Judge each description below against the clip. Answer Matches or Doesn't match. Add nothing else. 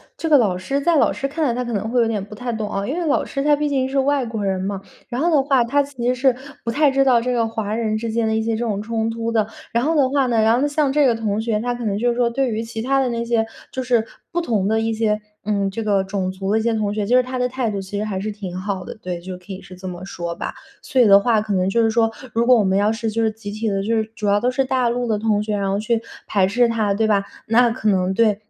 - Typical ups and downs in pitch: Matches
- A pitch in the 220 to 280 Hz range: Matches